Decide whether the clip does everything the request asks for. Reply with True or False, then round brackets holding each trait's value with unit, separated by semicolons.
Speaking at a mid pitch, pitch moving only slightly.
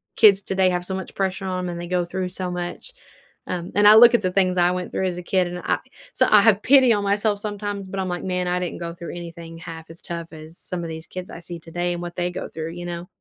True (180 Hz; 1.9 semitones)